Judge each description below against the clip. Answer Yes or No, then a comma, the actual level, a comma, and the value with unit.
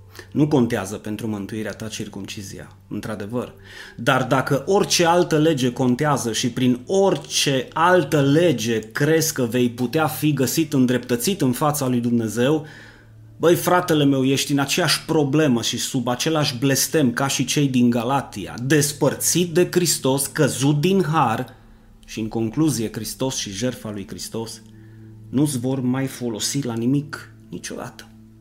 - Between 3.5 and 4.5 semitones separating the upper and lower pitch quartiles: No, average, 5.1 semitones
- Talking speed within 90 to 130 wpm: No, average, 140 wpm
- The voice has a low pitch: Yes, low, 125 Hz